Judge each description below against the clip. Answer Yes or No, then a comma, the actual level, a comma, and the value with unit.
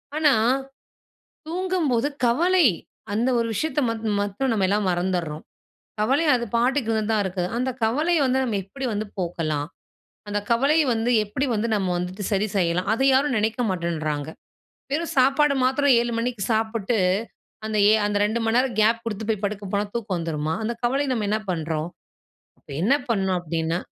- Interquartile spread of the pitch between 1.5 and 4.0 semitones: No, average, 5.3 semitones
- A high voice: Yes, high, 220 Hz